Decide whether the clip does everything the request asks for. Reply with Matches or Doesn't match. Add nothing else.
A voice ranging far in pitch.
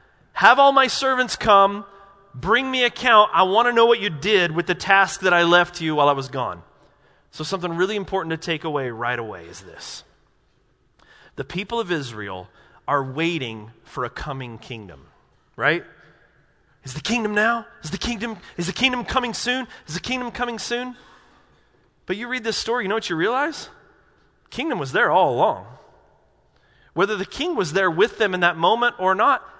Matches